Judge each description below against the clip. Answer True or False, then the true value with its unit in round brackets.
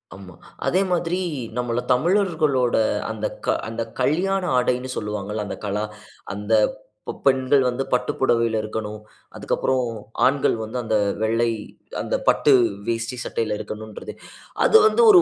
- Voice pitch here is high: False (120 Hz)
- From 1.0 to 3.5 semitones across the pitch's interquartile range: False (4.0 semitones)